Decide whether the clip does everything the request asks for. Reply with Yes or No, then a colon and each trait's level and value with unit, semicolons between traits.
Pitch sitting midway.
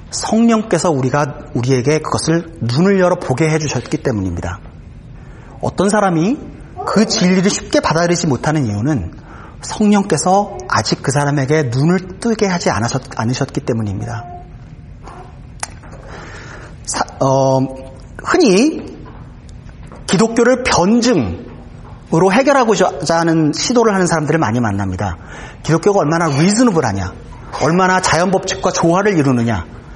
Yes: medium, 160 Hz